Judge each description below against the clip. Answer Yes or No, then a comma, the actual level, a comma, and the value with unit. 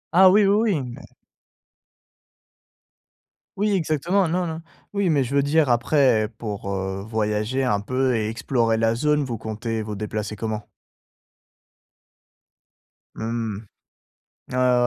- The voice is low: Yes, low, 120 Hz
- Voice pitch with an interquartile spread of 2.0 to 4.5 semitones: No, wide, 5.6 semitones